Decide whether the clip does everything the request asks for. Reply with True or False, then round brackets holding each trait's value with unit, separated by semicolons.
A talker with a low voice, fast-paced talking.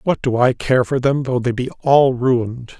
True (125 Hz; 235 wpm)